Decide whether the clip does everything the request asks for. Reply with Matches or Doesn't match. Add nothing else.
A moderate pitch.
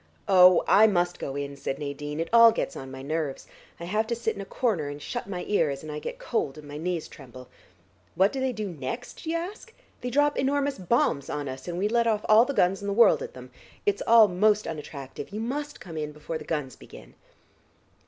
Matches